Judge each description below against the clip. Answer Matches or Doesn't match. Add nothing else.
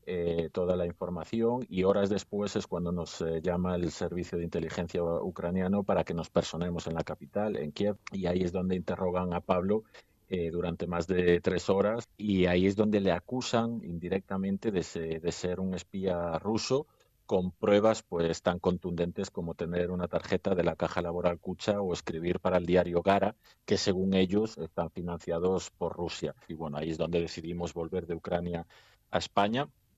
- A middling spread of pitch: Doesn't match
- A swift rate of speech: Doesn't match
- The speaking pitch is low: Matches